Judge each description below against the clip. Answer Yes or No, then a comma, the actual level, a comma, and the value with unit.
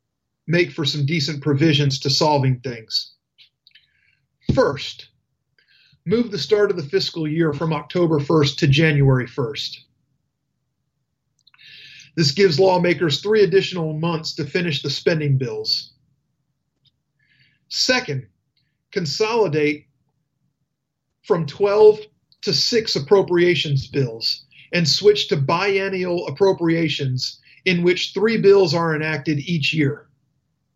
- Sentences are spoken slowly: Yes, slow, 105 wpm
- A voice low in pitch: No, medium, 150 Hz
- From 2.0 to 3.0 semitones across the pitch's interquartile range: No, average, 3.9 semitones